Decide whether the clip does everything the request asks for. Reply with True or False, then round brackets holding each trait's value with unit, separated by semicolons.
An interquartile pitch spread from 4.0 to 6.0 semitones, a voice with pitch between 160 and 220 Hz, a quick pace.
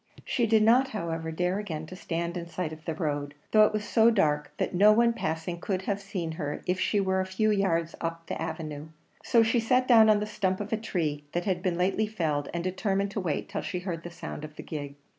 True (4.4 semitones; 185 Hz; 245 wpm)